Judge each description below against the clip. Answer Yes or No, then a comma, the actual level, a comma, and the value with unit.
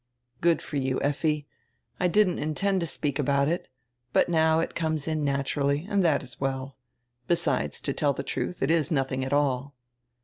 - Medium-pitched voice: Yes, medium, 145 Hz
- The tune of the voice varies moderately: Yes, average, 3.0 semitones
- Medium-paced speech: Yes, average, 180 wpm